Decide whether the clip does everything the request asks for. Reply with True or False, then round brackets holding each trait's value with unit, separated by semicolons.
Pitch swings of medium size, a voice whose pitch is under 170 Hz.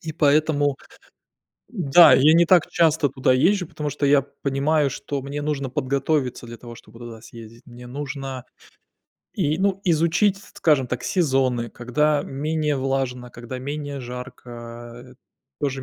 True (3.5 semitones; 140 Hz)